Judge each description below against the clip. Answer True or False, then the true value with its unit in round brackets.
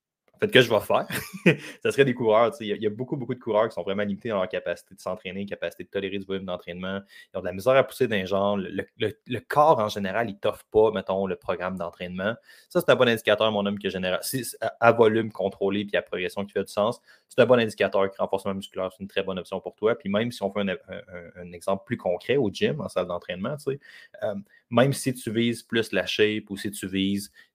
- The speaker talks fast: True (255 wpm)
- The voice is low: True (100 Hz)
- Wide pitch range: False (3.3 semitones)